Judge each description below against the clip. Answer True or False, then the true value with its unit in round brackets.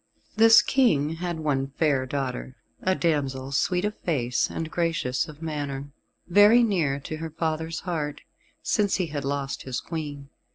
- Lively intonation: False (3.8 semitones)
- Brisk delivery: False (155 wpm)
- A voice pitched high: False (155 Hz)